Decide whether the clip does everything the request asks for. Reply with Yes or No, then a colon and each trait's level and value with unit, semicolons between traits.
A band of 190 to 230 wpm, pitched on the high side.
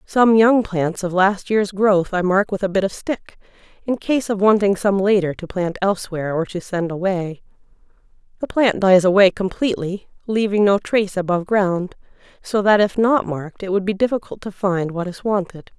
Yes: average, 195 wpm; high, 195 Hz